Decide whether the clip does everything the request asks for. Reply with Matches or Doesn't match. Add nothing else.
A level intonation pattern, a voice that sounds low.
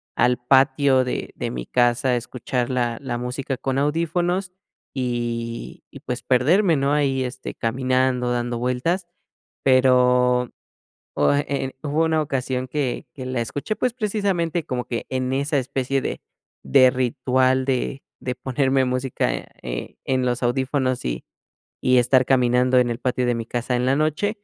Matches